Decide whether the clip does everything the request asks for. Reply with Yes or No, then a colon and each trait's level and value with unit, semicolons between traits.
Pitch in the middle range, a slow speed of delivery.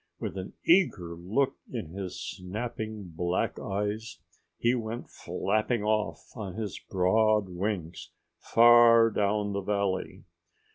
No: low, 105 Hz; slow, 115 wpm